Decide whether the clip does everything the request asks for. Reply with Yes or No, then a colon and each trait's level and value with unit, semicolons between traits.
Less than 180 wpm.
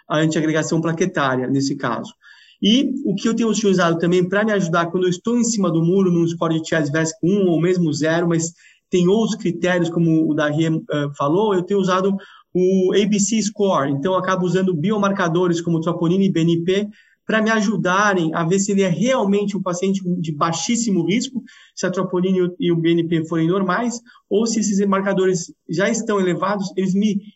No: average, 185 wpm